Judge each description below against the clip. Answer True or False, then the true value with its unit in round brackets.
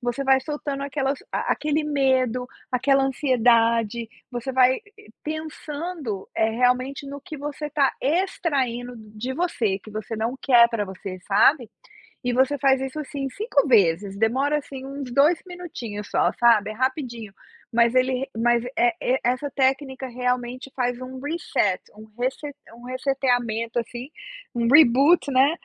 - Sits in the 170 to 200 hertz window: False (255 Hz)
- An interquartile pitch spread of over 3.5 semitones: False (3.1 semitones)